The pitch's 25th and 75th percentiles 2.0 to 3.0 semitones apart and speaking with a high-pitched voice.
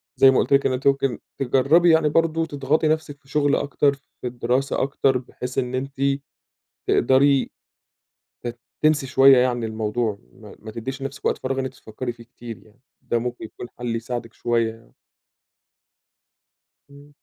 No: average, 2.7 semitones; low, 130 Hz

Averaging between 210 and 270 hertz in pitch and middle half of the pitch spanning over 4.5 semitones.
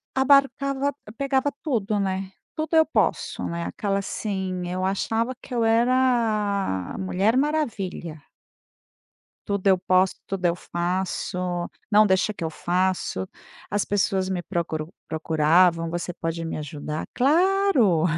No: high, 195 Hz; wide, 5.5 semitones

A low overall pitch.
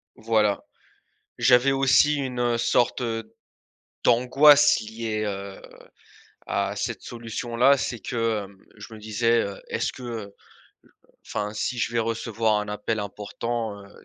Yes: low, 115 Hz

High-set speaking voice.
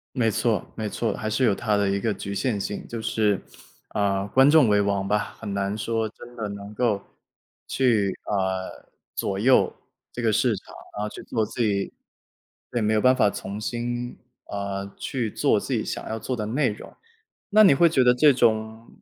No: low, 110 Hz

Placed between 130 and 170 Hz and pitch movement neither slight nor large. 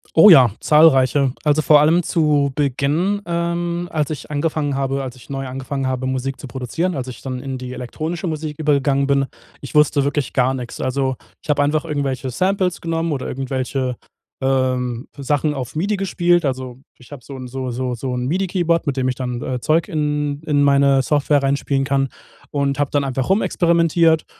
Yes: medium, 140 Hz; average, 3.1 semitones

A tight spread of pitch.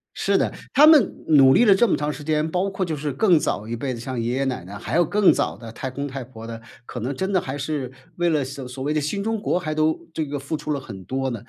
No: average, 4.6 semitones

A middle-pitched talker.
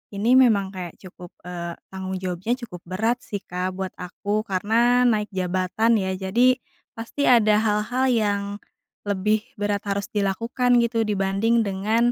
No: high, 205 Hz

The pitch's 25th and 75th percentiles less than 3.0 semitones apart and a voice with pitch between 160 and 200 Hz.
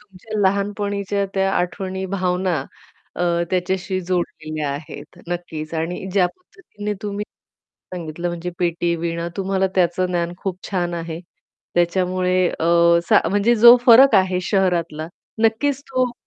Yes: narrow, 2.6 semitones; medium, 185 Hz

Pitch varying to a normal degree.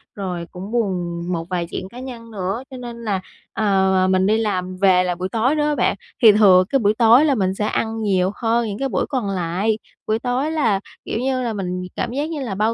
Yes: average, 4.5 semitones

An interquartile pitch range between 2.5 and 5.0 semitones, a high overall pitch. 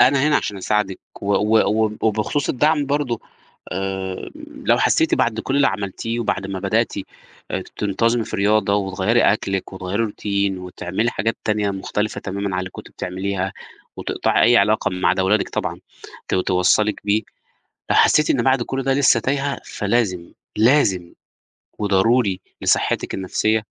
No: average, 3.4 semitones; low, 105 Hz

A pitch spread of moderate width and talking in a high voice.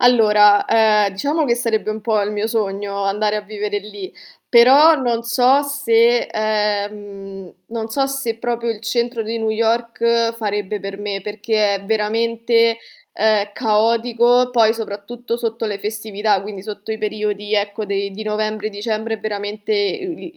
No: narrow, 2.0 semitones; high, 215 Hz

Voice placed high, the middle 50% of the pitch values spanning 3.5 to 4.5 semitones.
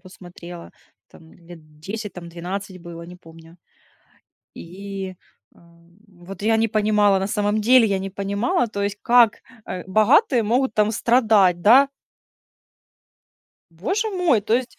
Yes: high, 200 Hz; average, 4.0 semitones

